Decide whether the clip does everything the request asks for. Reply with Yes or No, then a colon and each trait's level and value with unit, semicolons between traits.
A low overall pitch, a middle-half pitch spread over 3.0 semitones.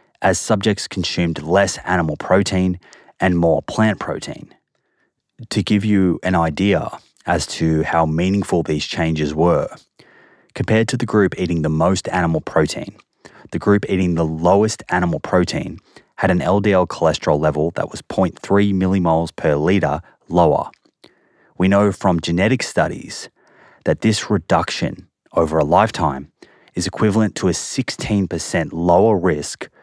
Yes: very low, 90 Hz; average, 3.6 semitones